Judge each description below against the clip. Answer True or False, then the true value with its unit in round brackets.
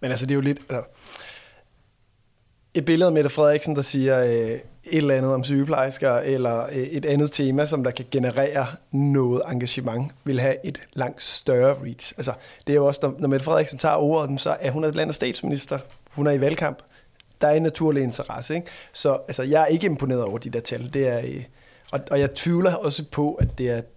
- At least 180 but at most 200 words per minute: False (220 wpm)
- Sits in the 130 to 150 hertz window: True (140 Hz)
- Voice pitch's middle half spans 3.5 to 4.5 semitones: False (2.6 semitones)